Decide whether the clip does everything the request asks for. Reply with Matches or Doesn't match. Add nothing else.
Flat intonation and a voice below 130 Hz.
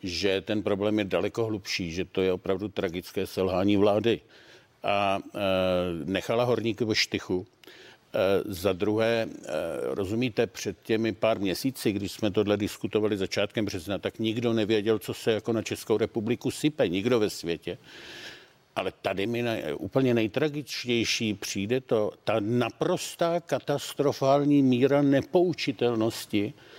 Doesn't match